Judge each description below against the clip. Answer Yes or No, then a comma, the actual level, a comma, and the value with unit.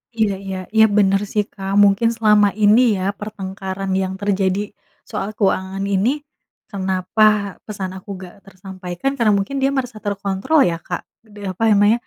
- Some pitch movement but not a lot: No, narrow, 1.9 semitones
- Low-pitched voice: No, high, 195 Hz